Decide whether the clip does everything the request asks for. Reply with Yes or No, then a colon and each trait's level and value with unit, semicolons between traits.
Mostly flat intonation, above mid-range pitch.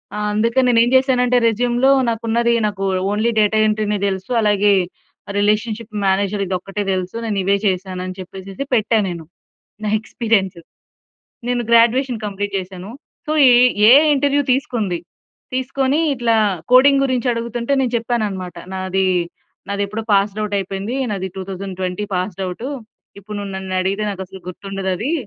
No: average, 3.7 semitones; high, 210 Hz